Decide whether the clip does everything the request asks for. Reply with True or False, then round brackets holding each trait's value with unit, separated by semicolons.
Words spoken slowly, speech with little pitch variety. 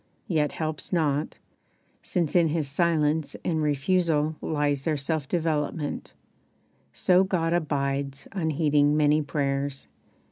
True (110 wpm; 2.3 semitones)